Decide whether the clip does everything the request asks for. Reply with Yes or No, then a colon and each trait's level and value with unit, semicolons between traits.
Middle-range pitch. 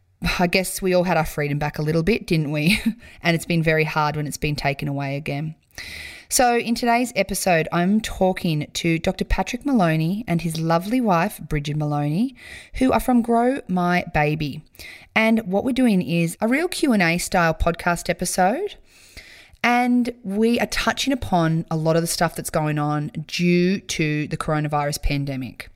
Yes: medium, 175 Hz